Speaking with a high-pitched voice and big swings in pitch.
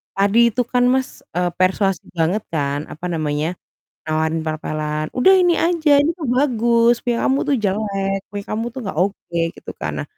Yes: high, 195 Hz; wide, 7.0 semitones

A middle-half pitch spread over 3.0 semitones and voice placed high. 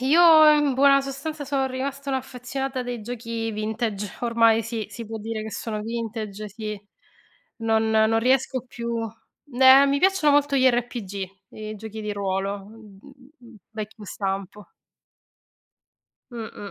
Yes: average, 3.7 semitones; high, 230 Hz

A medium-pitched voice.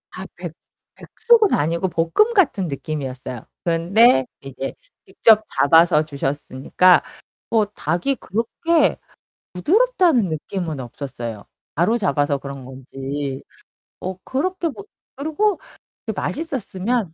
Yes: medium, 180 Hz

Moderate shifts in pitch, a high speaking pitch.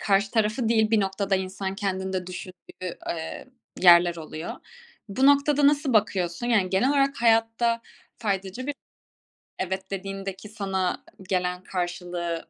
Yes: average, 3.7 semitones; high, 195 Hz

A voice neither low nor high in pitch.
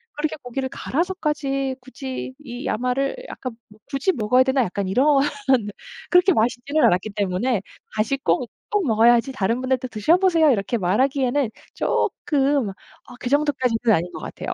No: very high, 255 Hz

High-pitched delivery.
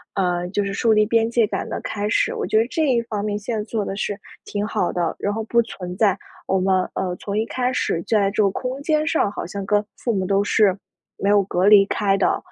Yes: high, 205 Hz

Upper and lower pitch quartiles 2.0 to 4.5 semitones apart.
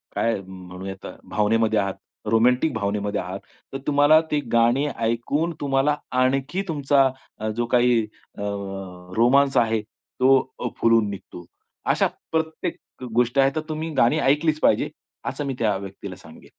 No: average, 5.0 semitones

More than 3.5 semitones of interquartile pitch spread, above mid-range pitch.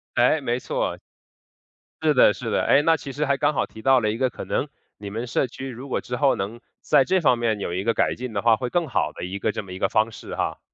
No: average, 4.1 semitones; low, 120 Hz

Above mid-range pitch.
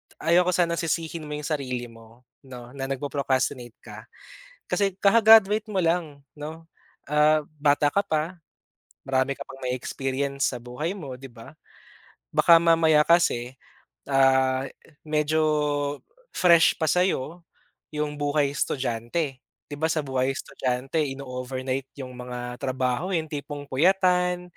No: medium, 145 Hz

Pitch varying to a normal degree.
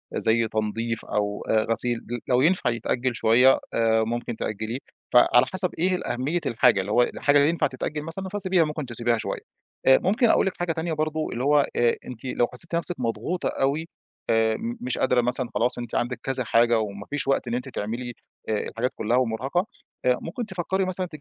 No: wide, 5.7 semitones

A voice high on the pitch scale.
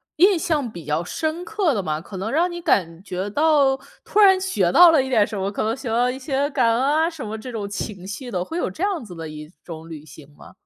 Yes: high, 245 Hz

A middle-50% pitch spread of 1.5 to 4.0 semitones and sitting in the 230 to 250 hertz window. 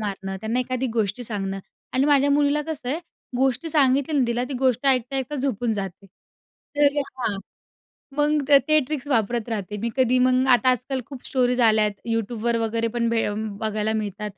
Yes: average, 3.7 semitones; high, 245 Hz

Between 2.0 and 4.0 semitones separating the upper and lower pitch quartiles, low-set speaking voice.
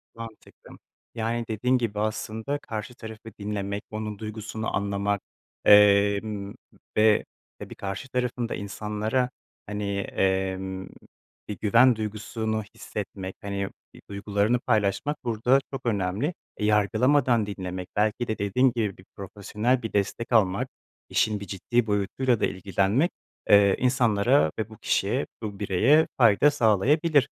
Yes: average, 2.9 semitones; low, 105 Hz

